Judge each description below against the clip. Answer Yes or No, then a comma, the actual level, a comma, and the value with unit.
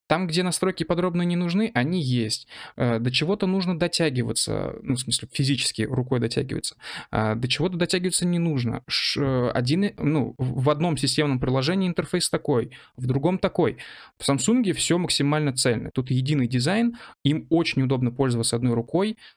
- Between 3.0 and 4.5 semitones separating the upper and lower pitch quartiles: No, wide, 5.5 semitones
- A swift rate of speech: No, average, 150 wpm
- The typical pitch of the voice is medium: Yes, medium, 145 Hz